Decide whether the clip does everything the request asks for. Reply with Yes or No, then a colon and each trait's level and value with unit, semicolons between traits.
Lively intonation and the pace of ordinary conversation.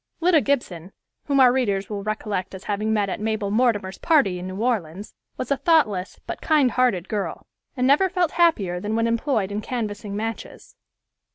No: average, 4.7 semitones; average, 180 wpm